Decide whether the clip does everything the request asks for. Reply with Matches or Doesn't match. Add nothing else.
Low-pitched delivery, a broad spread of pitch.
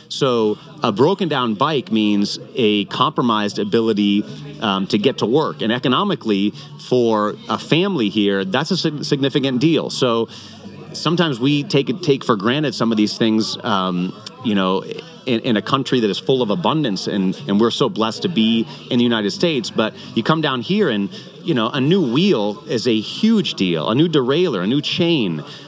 Matches